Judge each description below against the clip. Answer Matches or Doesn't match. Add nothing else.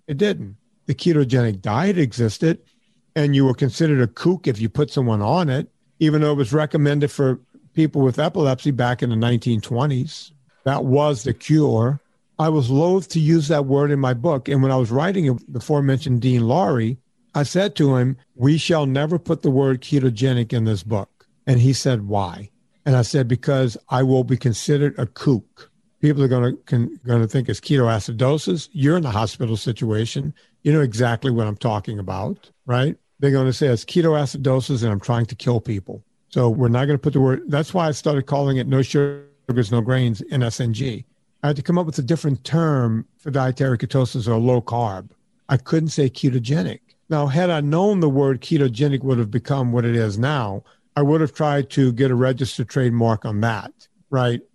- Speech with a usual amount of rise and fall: Matches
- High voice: Doesn't match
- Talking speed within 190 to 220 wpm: Matches